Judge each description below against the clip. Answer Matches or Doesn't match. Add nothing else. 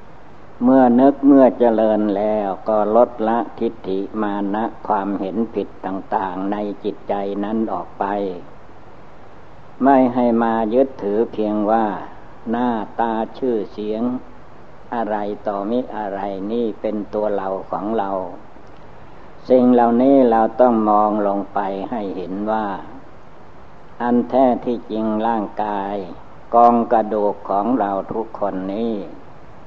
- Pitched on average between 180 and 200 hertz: Doesn't match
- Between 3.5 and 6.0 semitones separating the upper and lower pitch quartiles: Doesn't match